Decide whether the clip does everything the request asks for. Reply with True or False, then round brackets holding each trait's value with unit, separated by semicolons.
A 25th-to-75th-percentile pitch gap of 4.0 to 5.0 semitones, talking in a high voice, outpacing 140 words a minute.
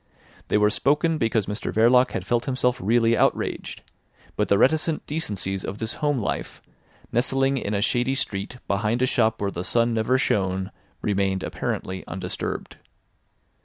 False (4.4 semitones; 115 Hz; 155 wpm)